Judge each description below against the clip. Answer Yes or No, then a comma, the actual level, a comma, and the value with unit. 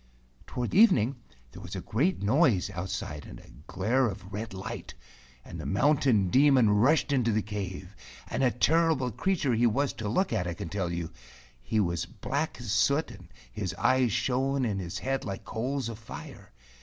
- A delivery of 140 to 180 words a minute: No, average, 190 wpm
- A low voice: Yes, low, 115 Hz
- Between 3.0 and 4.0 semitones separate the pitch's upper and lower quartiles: No, wide, 5.4 semitones